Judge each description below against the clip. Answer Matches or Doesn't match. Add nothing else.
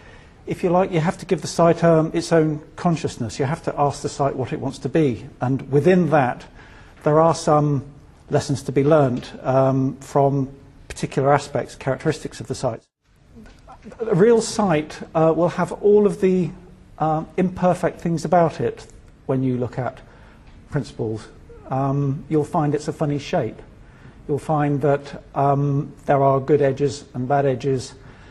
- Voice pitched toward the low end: Doesn't match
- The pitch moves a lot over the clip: Doesn't match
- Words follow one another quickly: Doesn't match